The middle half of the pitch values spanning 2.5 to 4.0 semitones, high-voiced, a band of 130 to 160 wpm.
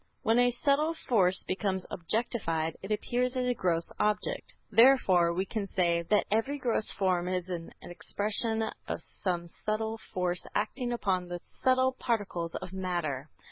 No: average, 5.1 semitones; high, 200 Hz; average, 150 wpm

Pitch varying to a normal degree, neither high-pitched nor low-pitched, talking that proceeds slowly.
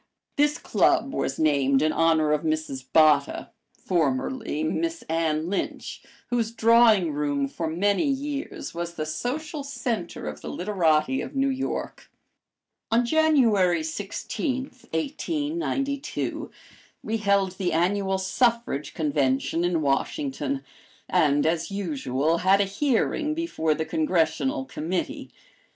No: wide, 8.5 semitones; medium, 180 Hz; slow, 120 wpm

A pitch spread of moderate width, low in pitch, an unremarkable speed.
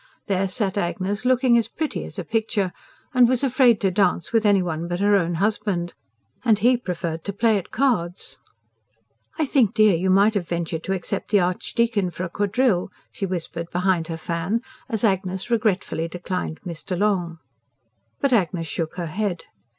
No: average, 4.0 semitones; high, 195 Hz; average, 175 wpm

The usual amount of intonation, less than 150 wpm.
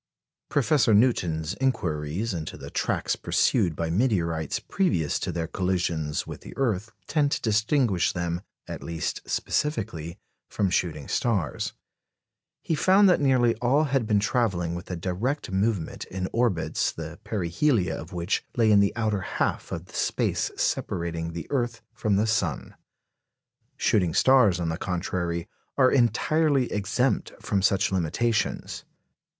No: wide, 6.1 semitones; average, 140 wpm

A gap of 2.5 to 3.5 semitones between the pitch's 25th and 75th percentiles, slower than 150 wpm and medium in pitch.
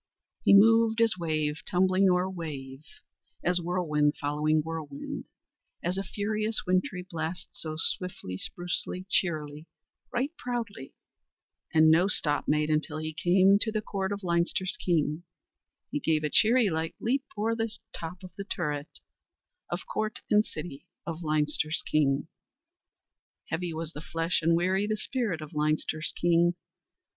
No: average, 4.0 semitones; average, 140 wpm; medium, 170 Hz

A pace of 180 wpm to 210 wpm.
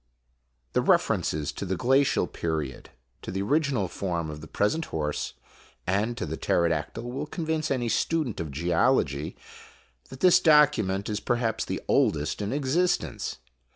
No: average, 150 wpm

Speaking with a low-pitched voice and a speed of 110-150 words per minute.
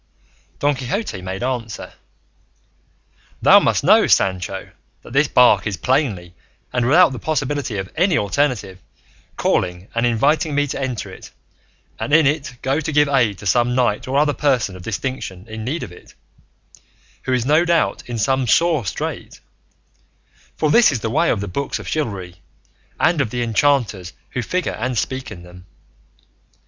No: low, 125 Hz; average, 165 wpm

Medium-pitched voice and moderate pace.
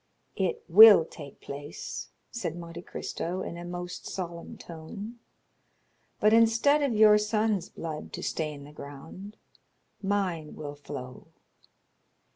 No: medium, 175 Hz; slow, 120 wpm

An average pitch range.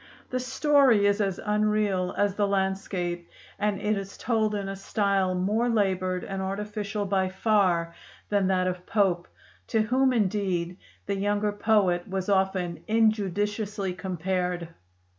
No: narrow, 2.2 semitones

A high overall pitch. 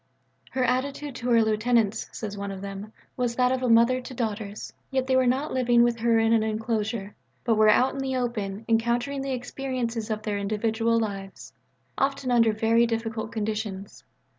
Yes: high, 230 Hz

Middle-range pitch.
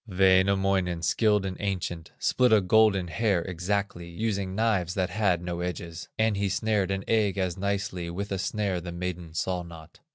No: very low, 95 Hz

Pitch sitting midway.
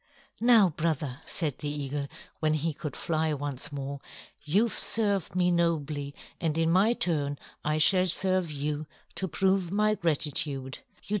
Yes: medium, 155 Hz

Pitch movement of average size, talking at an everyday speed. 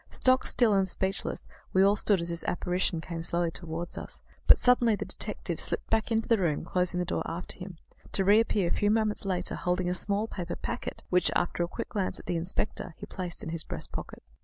No: average, 3.1 semitones; fast, 220 wpm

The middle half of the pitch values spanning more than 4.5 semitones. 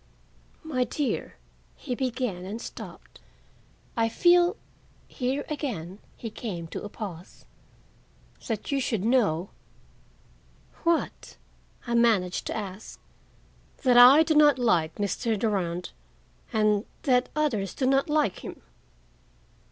Yes: average, 5.2 semitones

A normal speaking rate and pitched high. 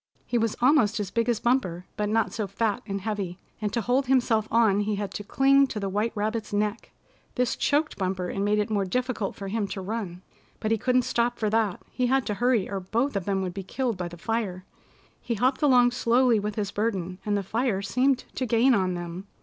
No: fast, 230 wpm; high, 215 Hz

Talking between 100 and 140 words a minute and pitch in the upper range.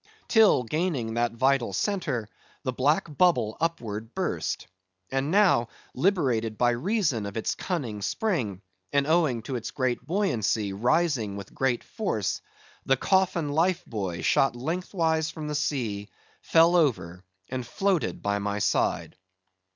No: slow, 135 wpm; low, 130 Hz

